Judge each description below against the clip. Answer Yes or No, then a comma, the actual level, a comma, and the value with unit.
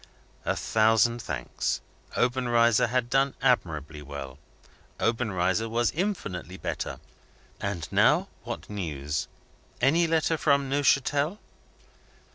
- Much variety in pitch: Yes, wide, 6.9 semitones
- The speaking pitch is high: No, low, 115 Hz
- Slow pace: Yes, slow, 95 wpm